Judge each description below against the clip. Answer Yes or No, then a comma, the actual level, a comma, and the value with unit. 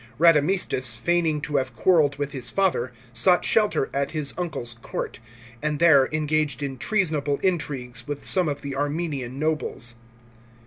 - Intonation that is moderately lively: Yes, average, 3.5 semitones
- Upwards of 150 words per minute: No, average, 145 wpm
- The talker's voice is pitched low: No, medium, 145 Hz